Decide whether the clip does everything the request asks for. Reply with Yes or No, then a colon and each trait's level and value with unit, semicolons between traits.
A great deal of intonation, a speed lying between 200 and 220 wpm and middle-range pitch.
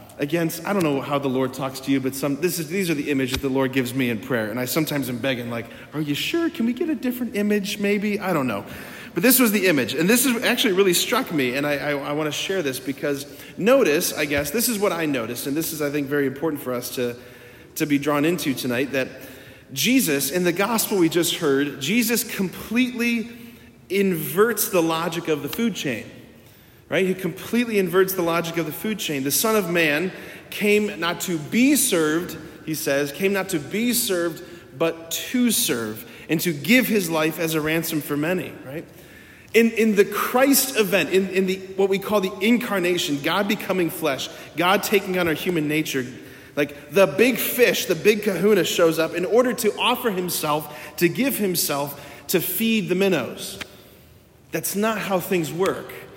Yes: wide, 6.1 semitones; fast, 205 wpm; medium, 170 Hz